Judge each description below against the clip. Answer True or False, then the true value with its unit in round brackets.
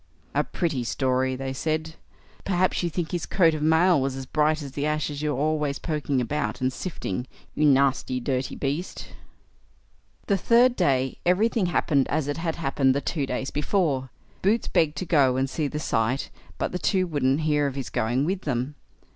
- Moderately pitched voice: True (150 Hz)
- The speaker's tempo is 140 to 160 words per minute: False (190 wpm)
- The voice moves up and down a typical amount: True (3.6 semitones)